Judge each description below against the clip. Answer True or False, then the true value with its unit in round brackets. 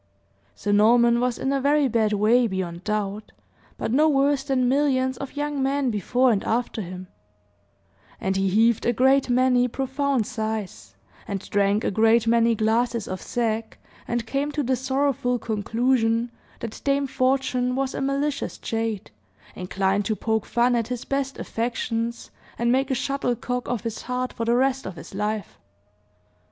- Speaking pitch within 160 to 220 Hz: False (240 Hz)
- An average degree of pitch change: True (3.4 semitones)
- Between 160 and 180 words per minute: True (165 wpm)